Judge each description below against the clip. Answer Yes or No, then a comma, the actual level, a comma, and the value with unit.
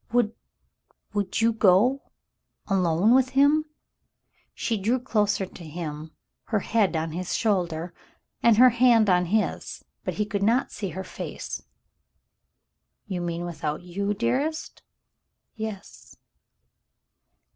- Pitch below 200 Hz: No, high, 205 Hz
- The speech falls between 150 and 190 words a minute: No, slow, 135 wpm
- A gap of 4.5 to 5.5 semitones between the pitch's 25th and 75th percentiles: Yes, average, 4.8 semitones